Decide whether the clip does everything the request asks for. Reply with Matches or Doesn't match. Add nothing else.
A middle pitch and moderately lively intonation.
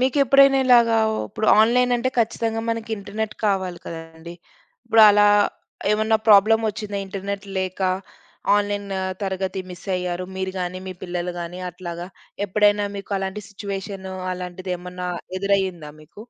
Doesn't match